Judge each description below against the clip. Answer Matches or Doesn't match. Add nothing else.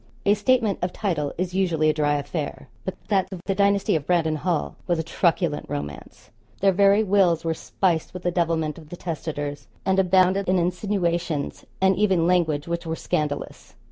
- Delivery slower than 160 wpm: Doesn't match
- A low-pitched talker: Doesn't match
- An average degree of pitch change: Matches